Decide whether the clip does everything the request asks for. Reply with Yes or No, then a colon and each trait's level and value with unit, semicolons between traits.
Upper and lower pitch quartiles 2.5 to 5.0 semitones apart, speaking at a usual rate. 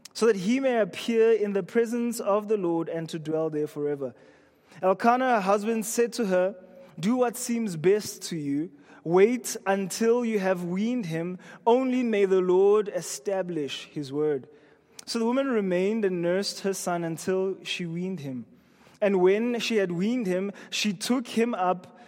Yes: average, 4.5 semitones; average, 170 wpm